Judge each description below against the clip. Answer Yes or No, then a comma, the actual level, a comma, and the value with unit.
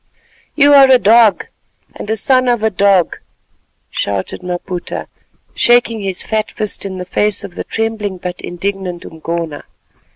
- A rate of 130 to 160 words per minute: Yes, average, 150 wpm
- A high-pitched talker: Yes, high, 200 Hz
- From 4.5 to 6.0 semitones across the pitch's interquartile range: No, average, 3.8 semitones